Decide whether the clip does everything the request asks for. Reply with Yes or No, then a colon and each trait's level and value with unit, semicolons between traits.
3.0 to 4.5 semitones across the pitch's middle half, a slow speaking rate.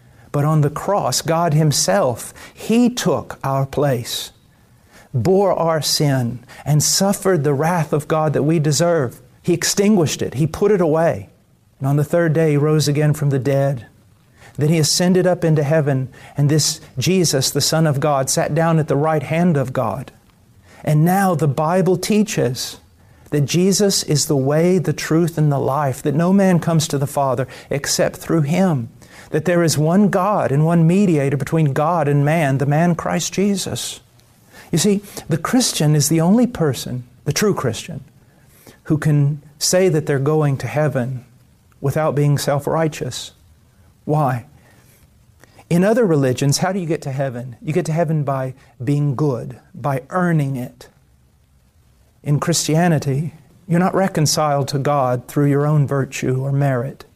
No: average, 3.5 semitones; average, 165 wpm